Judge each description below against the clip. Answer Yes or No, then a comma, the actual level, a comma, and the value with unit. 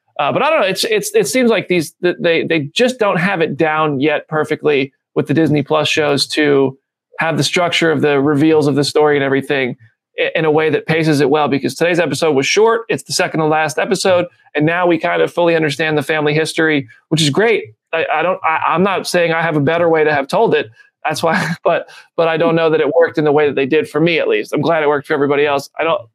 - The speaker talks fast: Yes, fast, 260 wpm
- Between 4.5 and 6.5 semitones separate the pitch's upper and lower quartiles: No, narrow, 2.6 semitones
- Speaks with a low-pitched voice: No, medium, 155 Hz